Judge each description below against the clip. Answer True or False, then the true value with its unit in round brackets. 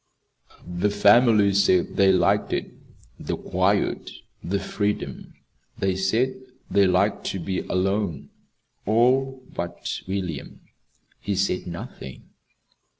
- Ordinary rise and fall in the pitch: False (2.3 semitones)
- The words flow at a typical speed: False (105 wpm)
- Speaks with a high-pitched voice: False (100 Hz)